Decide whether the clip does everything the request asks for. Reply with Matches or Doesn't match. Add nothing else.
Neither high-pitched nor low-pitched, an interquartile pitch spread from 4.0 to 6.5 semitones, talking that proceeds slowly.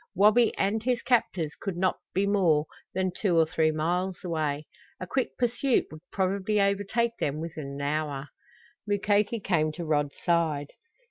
Doesn't match